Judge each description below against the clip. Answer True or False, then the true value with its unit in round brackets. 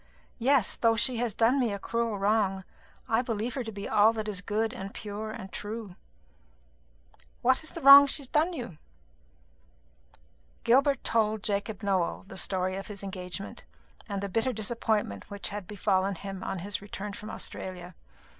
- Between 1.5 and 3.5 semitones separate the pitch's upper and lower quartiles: True (2.9 semitones)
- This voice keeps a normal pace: True (175 wpm)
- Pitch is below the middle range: False (210 Hz)